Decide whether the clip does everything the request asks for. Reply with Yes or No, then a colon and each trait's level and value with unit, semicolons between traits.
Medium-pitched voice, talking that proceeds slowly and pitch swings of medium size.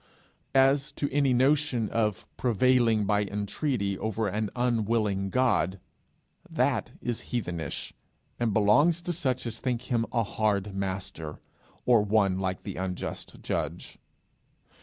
No: low, 110 Hz; slow, 125 wpm; average, 4.3 semitones